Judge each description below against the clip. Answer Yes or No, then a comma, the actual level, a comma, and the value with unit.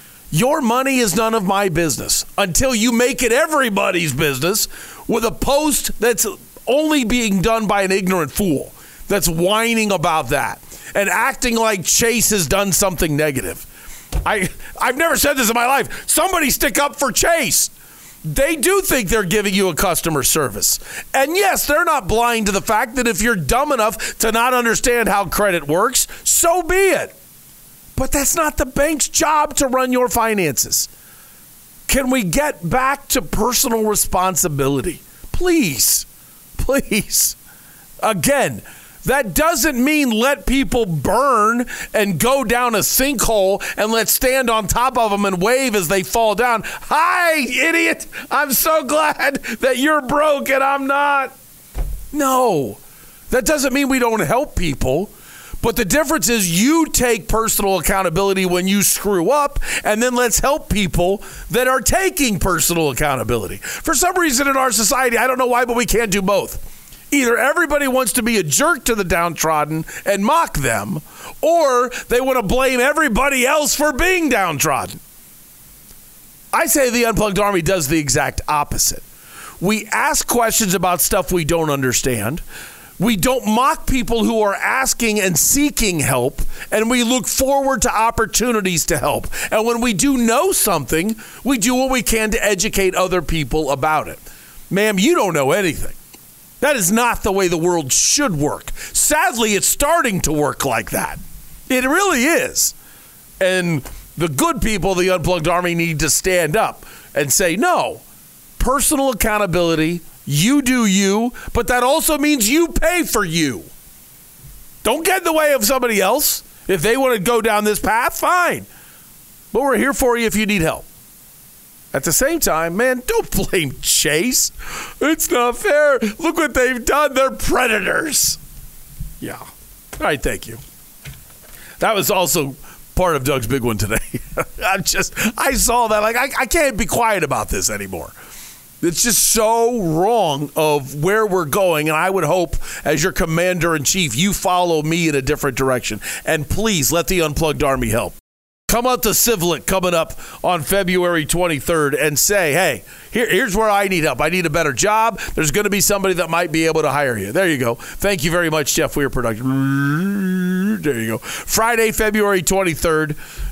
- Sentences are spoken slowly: No, average, 170 wpm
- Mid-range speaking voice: No, high, 220 Hz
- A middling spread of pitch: No, wide, 6.8 semitones